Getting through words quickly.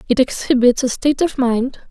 No: average, 190 wpm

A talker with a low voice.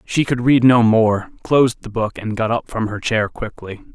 Yes: low, 115 Hz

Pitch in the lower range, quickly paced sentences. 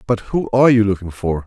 Yes: low, 105 Hz; fast, 245 wpm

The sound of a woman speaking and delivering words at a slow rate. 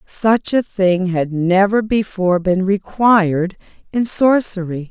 Yes: female; slow, 120 wpm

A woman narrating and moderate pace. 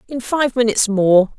Yes: female; average, 175 wpm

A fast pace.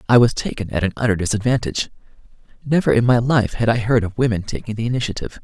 Yes: fast, 210 wpm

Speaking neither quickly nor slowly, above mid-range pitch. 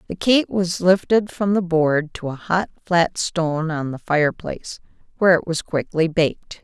No: average, 180 wpm; medium, 170 Hz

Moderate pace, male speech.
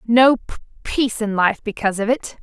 No: average, 175 wpm; female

